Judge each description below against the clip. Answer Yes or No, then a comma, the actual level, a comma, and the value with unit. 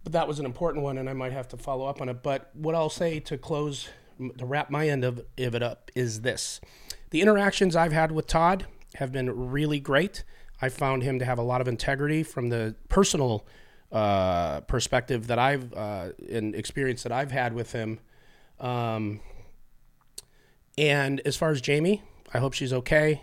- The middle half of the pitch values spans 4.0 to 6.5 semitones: No, average, 3.5 semitones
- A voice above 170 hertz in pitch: No, low, 135 Hz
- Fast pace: No, average, 195 wpm